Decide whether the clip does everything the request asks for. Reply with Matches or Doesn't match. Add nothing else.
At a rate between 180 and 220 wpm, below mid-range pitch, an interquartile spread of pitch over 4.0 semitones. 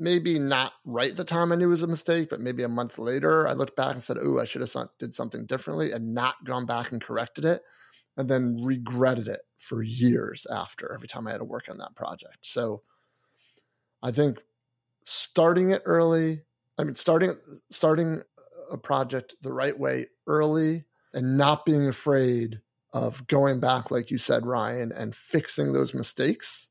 Matches